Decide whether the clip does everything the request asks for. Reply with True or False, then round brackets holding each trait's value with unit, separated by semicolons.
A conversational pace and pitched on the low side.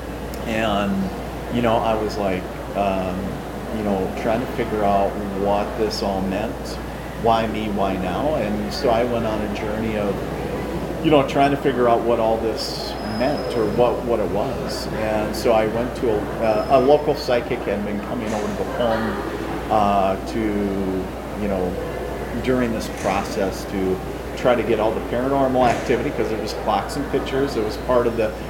True (180 wpm; 110 Hz)